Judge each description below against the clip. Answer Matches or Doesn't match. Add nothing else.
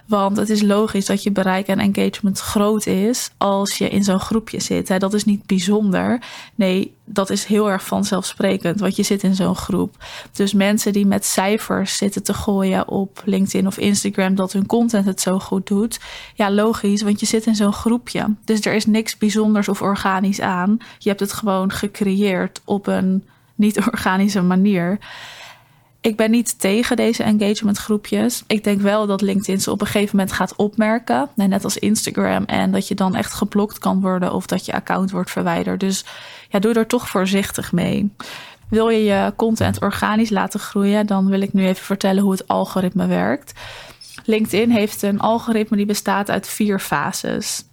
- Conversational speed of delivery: Matches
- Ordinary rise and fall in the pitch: Doesn't match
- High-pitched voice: Matches